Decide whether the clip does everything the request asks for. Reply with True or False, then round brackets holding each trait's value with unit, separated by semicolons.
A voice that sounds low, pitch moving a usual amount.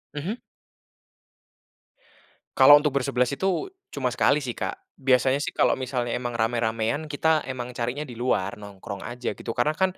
True (125 Hz; 3.5 semitones)